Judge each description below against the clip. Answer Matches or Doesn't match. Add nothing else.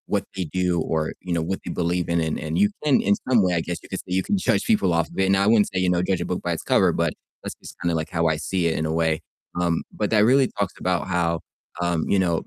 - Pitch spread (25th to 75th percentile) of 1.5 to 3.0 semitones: Matches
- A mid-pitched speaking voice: Doesn't match